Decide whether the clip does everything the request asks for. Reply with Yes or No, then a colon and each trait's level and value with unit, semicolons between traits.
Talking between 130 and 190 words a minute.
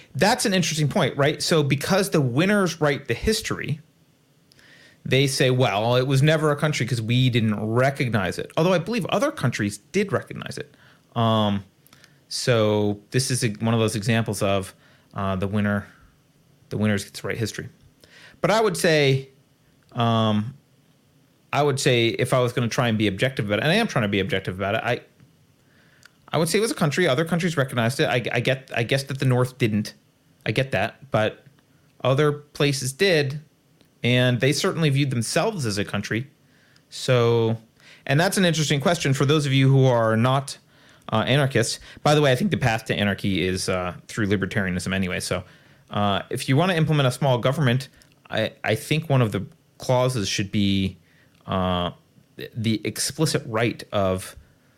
Yes: average, 185 wpm